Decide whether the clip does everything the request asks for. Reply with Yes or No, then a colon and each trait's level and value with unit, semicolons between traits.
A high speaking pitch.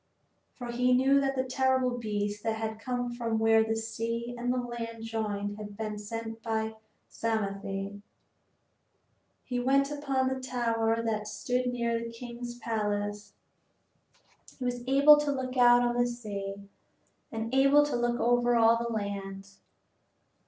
Yes: high, 235 Hz